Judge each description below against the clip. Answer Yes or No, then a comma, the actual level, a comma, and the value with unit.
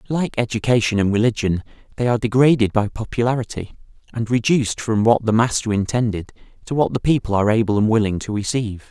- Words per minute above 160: Yes, average, 175 wpm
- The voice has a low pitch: Yes, low, 115 Hz